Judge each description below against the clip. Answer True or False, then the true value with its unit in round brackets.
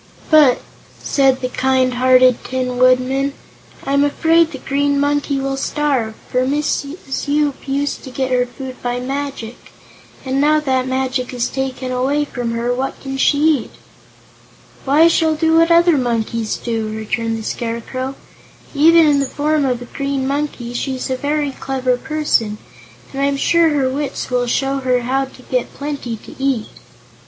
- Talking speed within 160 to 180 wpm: True (165 wpm)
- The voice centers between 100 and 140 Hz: False (270 Hz)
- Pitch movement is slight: True (2.3 semitones)